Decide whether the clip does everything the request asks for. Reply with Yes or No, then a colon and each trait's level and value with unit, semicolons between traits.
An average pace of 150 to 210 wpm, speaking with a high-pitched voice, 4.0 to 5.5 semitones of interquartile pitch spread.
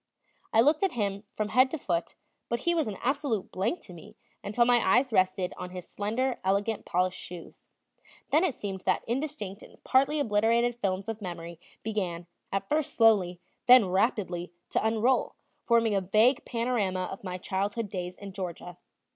Yes: average, 170 wpm; high, 210 Hz; average, 4.5 semitones